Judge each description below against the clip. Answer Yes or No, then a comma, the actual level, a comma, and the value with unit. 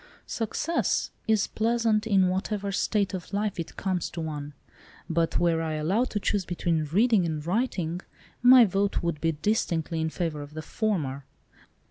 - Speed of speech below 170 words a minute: Yes, average, 160 wpm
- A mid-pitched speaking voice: Yes, medium, 180 Hz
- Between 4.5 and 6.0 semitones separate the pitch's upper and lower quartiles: Yes, average, 4.8 semitones